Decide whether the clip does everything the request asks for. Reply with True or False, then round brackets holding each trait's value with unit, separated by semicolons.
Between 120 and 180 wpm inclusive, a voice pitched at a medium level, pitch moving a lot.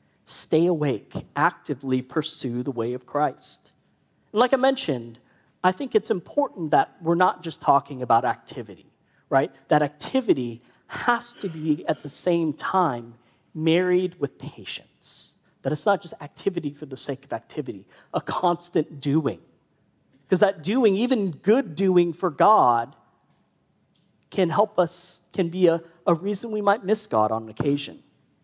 True (150 wpm; 170 Hz; 5.7 semitones)